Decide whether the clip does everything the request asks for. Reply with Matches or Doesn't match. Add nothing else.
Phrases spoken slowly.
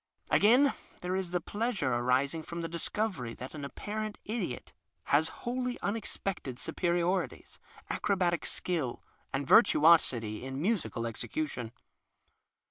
Matches